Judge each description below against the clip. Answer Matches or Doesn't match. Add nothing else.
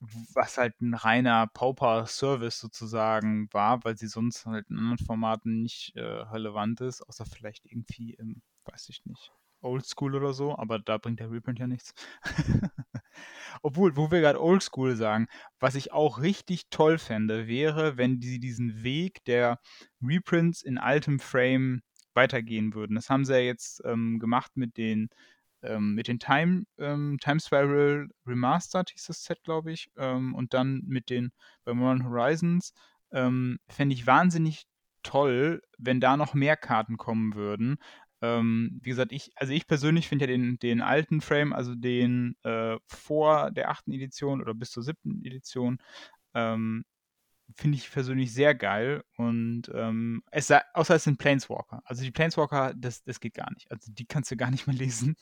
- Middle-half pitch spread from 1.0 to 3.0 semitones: Doesn't match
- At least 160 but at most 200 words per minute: Matches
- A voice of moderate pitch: Doesn't match